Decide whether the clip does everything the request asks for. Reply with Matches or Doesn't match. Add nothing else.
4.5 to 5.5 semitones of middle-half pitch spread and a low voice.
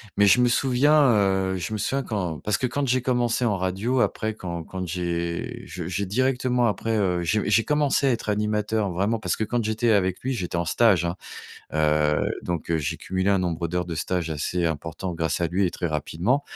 Matches